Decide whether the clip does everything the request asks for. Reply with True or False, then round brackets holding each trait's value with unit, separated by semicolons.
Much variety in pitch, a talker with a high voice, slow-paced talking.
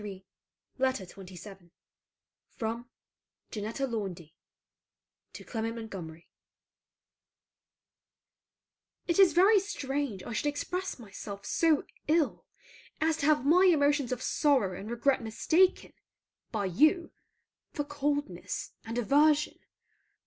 True (6.5 semitones; 255 Hz; 105 wpm)